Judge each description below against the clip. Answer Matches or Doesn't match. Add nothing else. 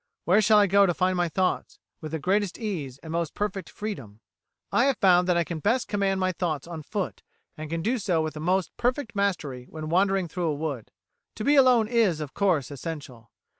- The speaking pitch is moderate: Matches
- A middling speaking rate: Doesn't match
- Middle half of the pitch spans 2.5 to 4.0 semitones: Doesn't match